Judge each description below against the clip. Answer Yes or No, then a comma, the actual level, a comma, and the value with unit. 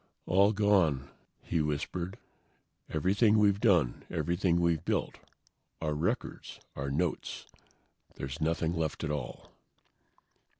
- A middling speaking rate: No, slow, 110 wpm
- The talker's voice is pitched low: Yes, very low, 85 Hz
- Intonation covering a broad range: No, average, 4.2 semitones